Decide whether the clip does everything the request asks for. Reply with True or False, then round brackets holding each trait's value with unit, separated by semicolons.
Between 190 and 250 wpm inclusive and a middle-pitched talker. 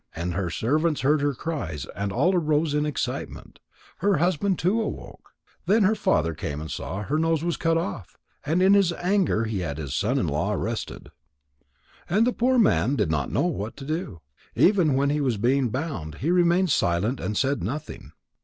True (195 wpm; 145 Hz)